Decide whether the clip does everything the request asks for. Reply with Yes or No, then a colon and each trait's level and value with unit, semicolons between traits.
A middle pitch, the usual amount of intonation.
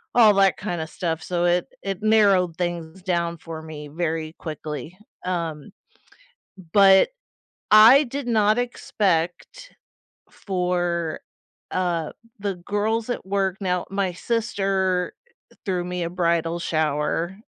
Yes: medium, 180 Hz; average, 3.0 semitones